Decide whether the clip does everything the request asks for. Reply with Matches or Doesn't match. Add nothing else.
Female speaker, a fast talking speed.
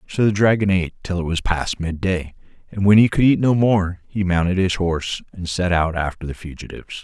Doesn't match